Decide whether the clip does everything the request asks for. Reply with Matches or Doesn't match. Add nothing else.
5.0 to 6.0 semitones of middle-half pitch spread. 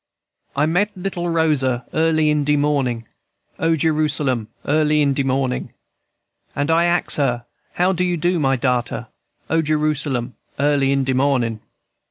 Doesn't match